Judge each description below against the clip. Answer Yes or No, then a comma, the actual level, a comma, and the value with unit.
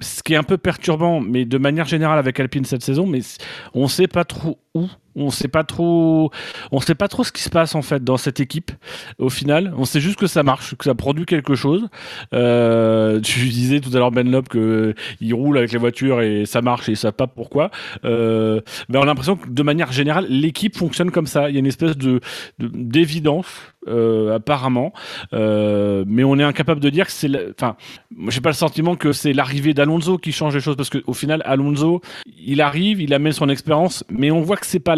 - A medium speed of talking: No, fast, 225 wpm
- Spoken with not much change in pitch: No, average, 4.4 semitones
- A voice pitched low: No, medium, 145 Hz